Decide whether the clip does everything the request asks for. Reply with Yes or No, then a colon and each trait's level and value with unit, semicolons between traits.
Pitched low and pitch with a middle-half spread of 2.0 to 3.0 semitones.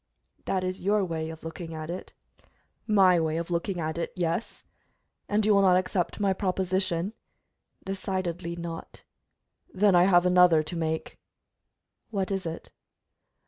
No: medium, 180 Hz; narrow, 2.4 semitones